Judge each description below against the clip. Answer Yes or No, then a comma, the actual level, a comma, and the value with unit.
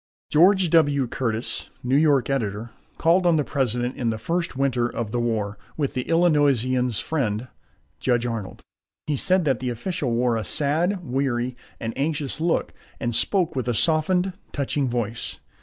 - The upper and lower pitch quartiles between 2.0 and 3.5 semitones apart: No, average, 4.8 semitones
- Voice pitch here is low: Yes, low, 130 Hz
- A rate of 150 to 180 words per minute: Yes, average, 160 wpm